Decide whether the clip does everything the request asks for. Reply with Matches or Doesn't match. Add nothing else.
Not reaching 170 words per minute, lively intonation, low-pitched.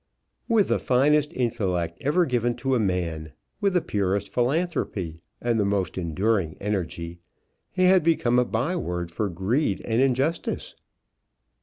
Matches